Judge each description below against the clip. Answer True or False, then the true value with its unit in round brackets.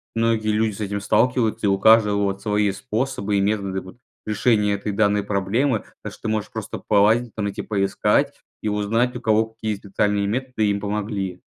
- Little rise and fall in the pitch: True (1.8 semitones)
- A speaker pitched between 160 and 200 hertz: False (105 Hz)